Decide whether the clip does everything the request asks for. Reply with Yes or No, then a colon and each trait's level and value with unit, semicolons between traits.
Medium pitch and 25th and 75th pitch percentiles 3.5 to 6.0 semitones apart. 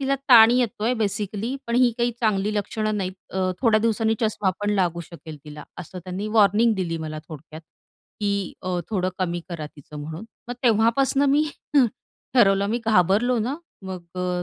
No: high, 205 Hz; average, 4.2 semitones